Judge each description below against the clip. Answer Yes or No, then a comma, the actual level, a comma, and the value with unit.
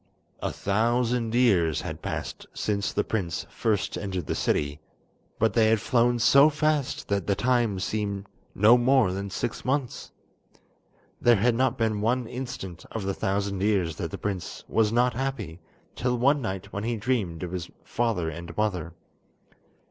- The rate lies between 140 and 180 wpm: Yes, average, 165 wpm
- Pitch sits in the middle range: No, low, 110 Hz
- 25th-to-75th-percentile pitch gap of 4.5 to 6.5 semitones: No, average, 4.0 semitones